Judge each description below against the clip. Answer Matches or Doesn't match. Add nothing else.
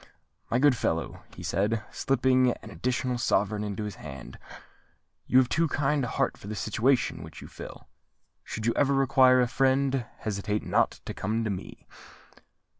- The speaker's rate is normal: Matches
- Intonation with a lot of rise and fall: Doesn't match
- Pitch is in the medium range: Doesn't match